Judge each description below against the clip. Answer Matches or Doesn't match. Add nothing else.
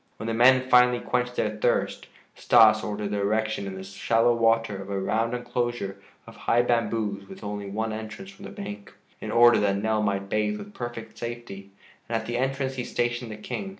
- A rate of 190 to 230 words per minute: Matches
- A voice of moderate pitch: Doesn't match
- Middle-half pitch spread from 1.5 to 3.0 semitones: Matches